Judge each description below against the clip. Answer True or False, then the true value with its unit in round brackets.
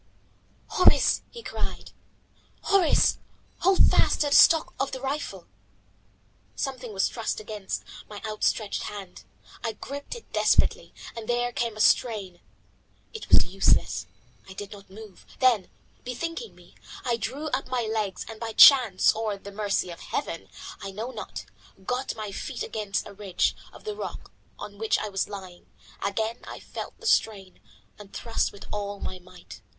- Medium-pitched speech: False (215 Hz)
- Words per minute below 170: True (160 wpm)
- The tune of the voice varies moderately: True (4.2 semitones)